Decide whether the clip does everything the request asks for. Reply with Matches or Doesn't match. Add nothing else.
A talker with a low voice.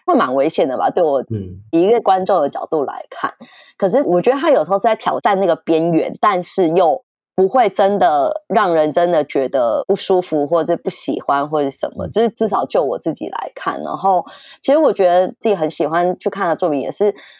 Doesn't match